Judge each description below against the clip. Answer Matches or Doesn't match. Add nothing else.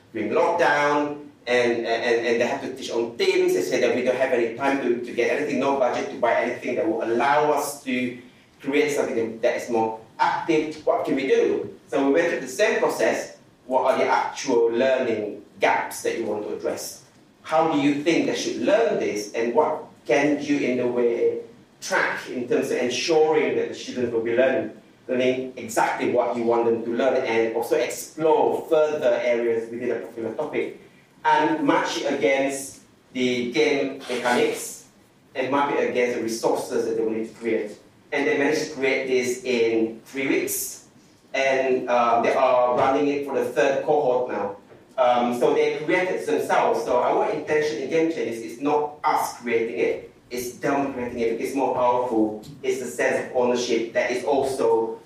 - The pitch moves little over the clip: Doesn't match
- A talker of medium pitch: Doesn't match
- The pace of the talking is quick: Doesn't match